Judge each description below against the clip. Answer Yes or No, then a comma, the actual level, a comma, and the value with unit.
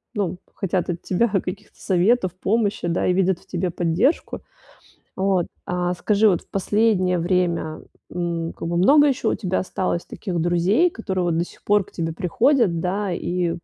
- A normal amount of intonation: Yes, average, 3.0 semitones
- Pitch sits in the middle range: Yes, medium, 180 Hz